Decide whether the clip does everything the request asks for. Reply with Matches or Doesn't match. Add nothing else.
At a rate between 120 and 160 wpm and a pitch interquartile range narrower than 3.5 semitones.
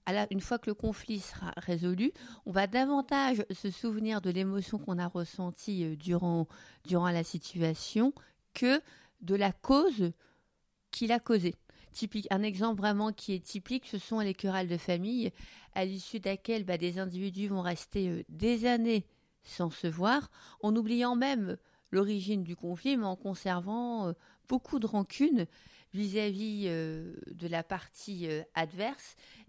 Doesn't match